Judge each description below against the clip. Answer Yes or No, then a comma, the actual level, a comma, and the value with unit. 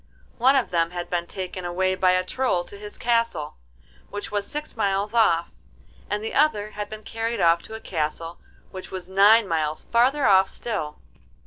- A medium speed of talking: Yes, average, 185 wpm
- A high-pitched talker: Yes, high, 195 Hz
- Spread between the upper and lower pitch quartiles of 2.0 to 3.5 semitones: No, average, 4.2 semitones